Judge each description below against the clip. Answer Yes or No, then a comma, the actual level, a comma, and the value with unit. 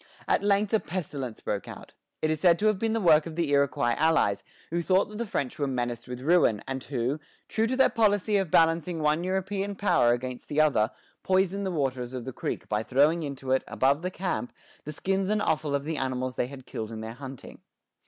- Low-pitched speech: No, medium, 155 Hz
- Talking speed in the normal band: No, fast, 220 wpm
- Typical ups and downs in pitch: No, wide, 6.5 semitones